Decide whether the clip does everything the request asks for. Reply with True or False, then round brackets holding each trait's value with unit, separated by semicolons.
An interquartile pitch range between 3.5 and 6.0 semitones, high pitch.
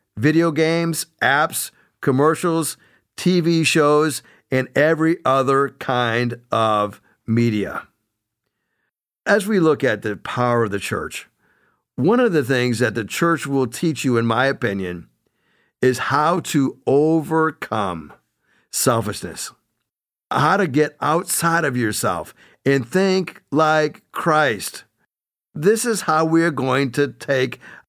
False (4.9 semitones; 140 Hz)